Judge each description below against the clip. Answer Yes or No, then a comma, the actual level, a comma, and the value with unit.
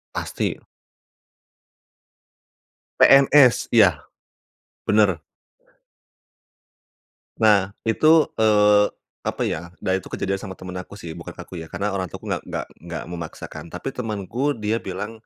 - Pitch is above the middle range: No, low, 105 Hz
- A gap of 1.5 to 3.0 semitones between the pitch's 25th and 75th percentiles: No, average, 3.6 semitones